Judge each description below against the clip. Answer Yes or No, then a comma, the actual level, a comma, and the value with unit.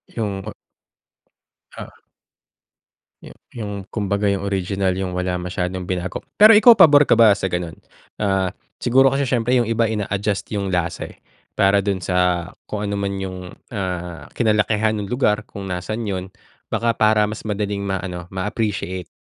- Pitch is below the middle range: Yes, low, 100 Hz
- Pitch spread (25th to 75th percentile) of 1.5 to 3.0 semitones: Yes, average, 2.7 semitones